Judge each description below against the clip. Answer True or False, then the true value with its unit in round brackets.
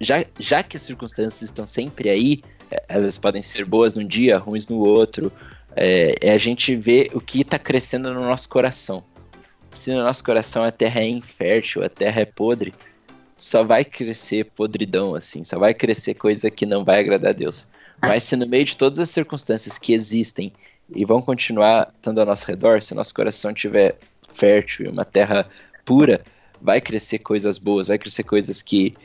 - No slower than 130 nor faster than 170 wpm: False (185 wpm)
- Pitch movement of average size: True (3.5 semitones)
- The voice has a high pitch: False (110 Hz)